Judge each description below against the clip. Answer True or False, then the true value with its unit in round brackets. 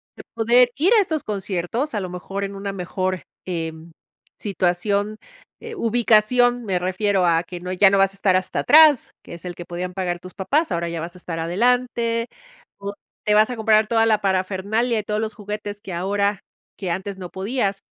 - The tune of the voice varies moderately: True (3.6 semitones)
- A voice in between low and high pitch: False (200 Hz)